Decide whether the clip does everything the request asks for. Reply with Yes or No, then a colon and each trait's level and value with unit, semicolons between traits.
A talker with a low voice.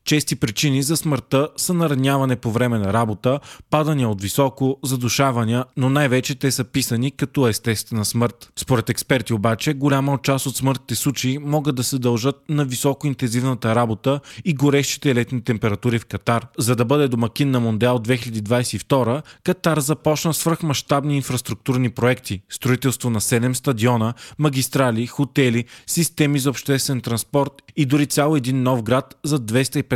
Yes: low, 130 Hz